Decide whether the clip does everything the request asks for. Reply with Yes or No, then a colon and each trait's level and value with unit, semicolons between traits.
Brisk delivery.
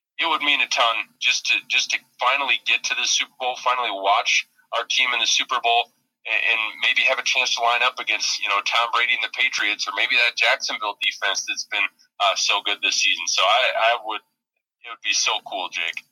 Yes: fast, 225 wpm